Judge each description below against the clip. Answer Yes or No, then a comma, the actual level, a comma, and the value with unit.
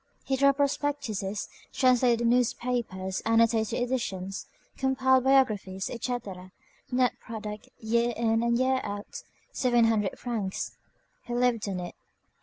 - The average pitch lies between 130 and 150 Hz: No, high, 235 Hz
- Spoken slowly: Yes, slow, 120 wpm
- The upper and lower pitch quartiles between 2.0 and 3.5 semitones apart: Yes, average, 3.2 semitones